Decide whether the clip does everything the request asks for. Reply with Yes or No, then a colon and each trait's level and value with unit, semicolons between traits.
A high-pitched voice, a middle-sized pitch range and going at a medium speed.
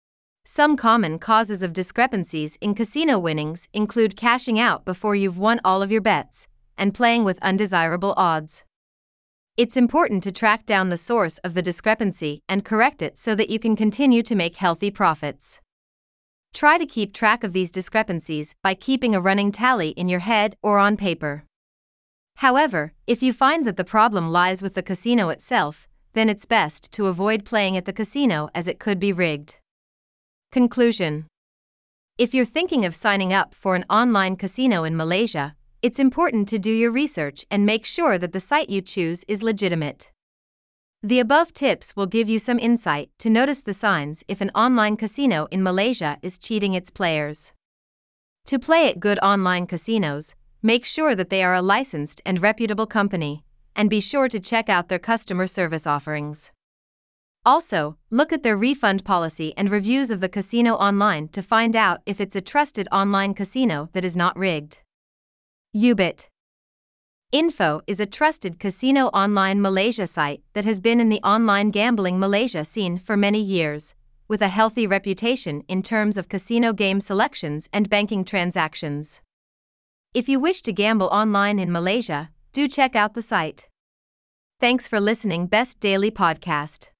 Yes: high, 200 Hz; average, 4.1 semitones; average, 170 wpm